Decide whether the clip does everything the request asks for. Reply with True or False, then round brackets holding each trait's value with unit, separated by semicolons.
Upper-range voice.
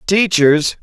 False (170 Hz)